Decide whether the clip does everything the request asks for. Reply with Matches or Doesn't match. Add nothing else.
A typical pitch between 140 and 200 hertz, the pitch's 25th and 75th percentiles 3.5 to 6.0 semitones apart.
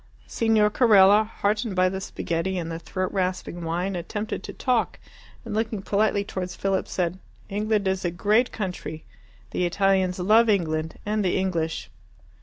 Doesn't match